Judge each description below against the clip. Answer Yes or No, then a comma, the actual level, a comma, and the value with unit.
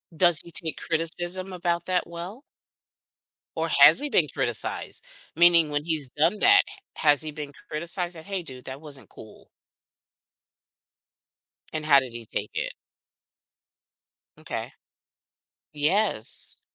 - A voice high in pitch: No, medium, 160 Hz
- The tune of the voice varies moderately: Yes, average, 3.2 semitones